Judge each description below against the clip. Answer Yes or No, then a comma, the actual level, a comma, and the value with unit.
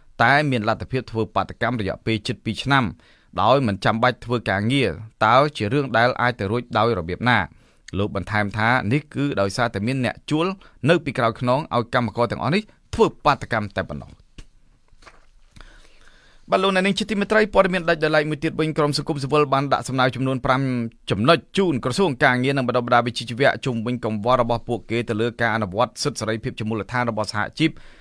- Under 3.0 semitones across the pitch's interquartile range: No, average, 3.9 semitones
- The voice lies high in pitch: No, low, 125 Hz